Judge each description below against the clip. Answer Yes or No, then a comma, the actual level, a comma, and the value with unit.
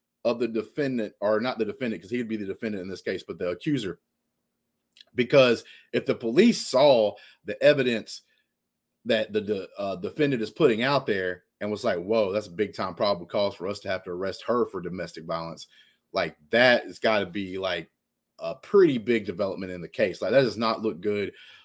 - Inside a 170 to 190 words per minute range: No, fast, 205 wpm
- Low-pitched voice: Yes, low, 110 Hz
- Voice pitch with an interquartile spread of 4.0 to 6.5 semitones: Yes, average, 4.3 semitones